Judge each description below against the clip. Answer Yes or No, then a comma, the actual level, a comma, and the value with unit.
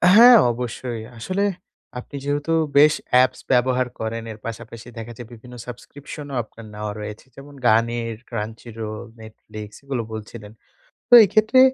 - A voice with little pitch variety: No, average, 3.8 semitones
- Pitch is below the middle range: Yes, low, 120 Hz